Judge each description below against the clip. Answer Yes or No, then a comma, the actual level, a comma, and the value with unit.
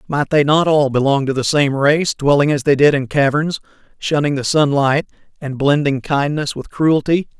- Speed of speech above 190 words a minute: No, average, 185 wpm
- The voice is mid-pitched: Yes, medium, 145 Hz